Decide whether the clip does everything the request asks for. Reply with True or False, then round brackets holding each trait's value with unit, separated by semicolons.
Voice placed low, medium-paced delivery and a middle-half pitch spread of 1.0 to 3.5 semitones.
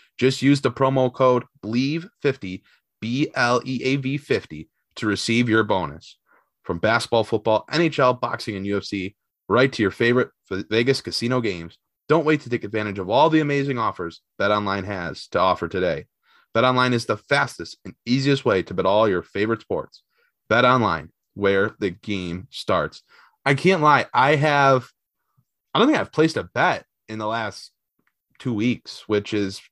False (120 Hz; 170 wpm; 4.7 semitones)